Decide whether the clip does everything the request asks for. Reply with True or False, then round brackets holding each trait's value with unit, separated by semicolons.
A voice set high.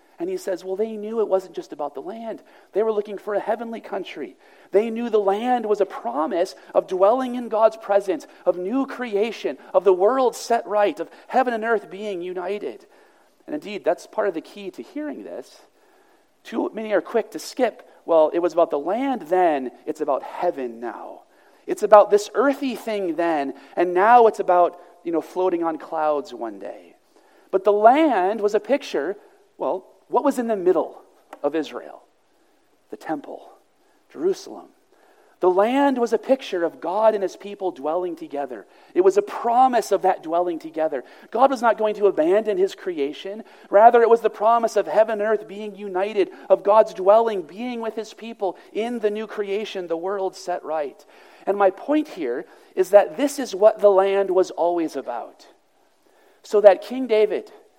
True (215 Hz)